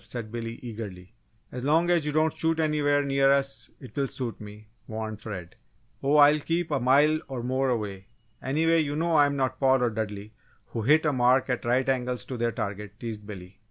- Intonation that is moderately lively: Yes, average, 4.8 semitones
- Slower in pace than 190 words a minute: No, fast, 205 wpm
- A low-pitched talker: Yes, low, 130 Hz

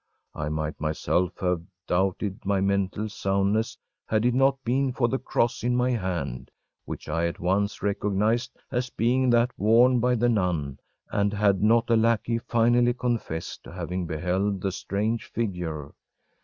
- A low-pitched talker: Yes, low, 105 Hz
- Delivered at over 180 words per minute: No, average, 155 wpm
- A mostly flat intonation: No, average, 4.6 semitones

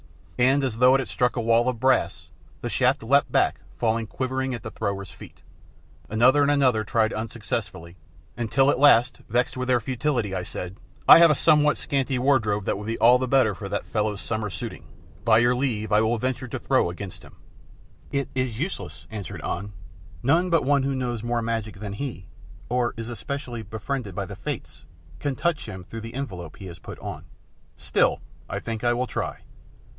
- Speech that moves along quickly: No, average, 195 wpm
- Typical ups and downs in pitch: Yes, average, 3.5 semitones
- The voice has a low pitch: Yes, low, 120 Hz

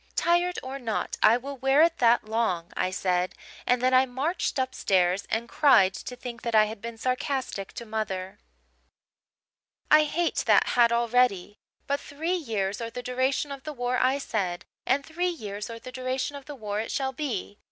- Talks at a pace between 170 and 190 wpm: Yes, average, 185 wpm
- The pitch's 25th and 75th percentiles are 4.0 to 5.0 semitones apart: Yes, average, 4.3 semitones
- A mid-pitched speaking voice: No, high, 245 Hz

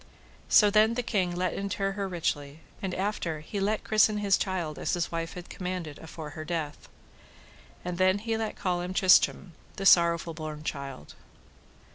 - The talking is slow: No, average, 170 wpm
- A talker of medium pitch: Yes, medium, 180 Hz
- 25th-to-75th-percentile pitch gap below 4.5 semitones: Yes, average, 3.5 semitones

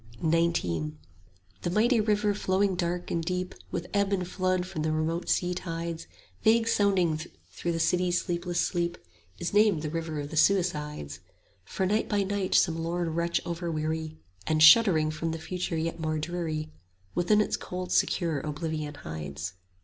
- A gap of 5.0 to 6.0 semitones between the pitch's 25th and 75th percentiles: No, average, 2.7 semitones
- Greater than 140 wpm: Yes, average, 165 wpm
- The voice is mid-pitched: Yes, medium, 170 Hz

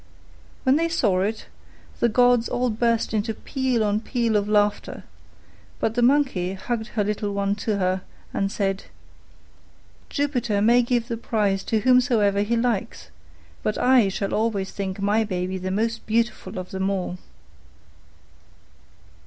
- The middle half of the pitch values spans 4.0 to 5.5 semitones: No, average, 3.2 semitones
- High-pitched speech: Yes, high, 215 Hz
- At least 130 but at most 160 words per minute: Yes, average, 145 wpm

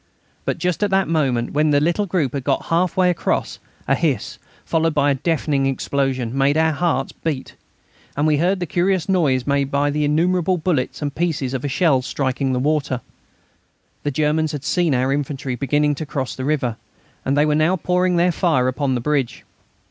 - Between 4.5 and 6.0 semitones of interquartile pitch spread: No, average, 3.6 semitones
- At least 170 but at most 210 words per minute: Yes, average, 190 wpm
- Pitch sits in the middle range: Yes, medium, 150 Hz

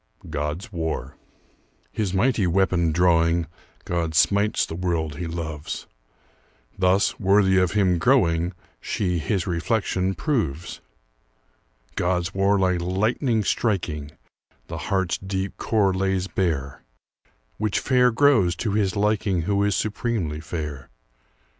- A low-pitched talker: Yes, very low, 95 Hz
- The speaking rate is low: Yes, slow, 115 wpm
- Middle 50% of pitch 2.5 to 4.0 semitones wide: Yes, average, 3.4 semitones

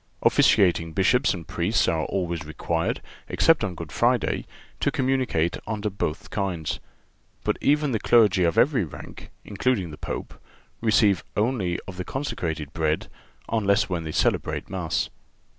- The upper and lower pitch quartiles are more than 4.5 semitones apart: Yes, wide, 5.5 semitones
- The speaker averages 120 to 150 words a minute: Yes, average, 140 wpm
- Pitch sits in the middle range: No, very low, 95 Hz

